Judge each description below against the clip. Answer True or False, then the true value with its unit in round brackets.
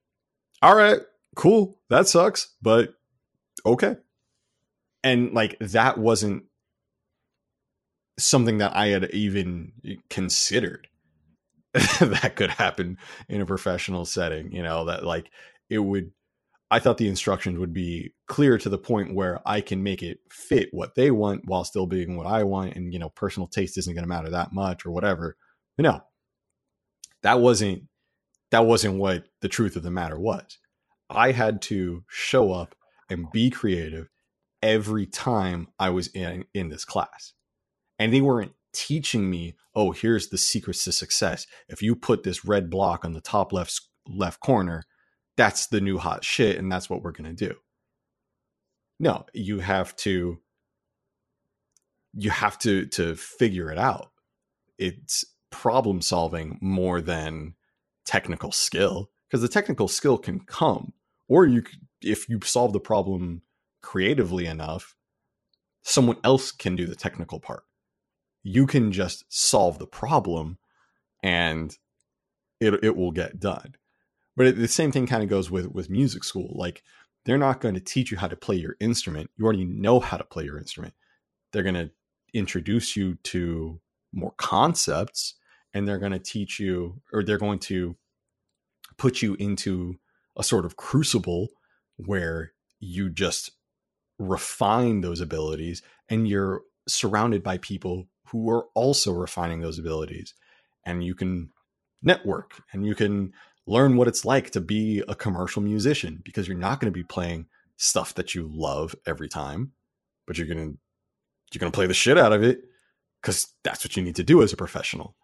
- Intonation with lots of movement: False (3.9 semitones)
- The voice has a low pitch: True (95 Hz)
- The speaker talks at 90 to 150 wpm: False (160 wpm)